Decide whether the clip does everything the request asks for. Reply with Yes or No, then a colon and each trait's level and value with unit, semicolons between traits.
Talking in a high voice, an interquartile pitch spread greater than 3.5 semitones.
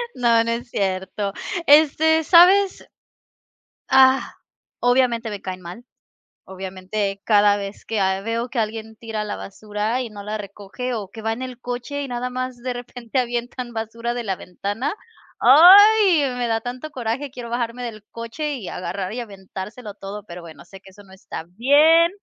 Yes: high, 230 Hz; average, 3.9 semitones